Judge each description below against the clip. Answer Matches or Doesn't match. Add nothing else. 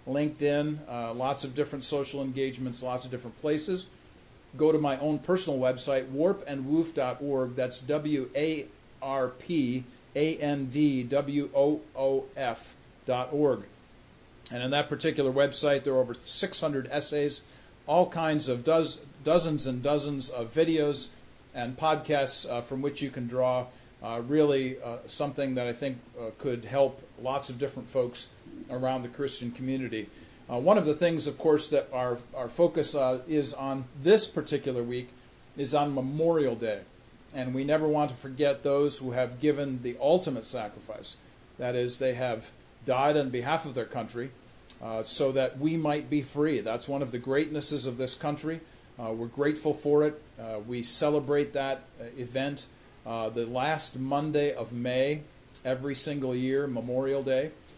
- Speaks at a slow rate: Doesn't match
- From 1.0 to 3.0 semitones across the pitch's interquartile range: Matches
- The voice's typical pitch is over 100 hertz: Matches